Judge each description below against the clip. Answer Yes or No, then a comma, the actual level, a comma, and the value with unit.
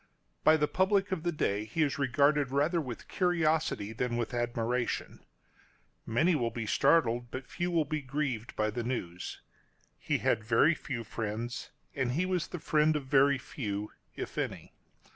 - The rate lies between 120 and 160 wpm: No, average, 170 wpm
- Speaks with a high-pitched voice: No, low, 135 Hz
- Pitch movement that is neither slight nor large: Yes, average, 4.9 semitones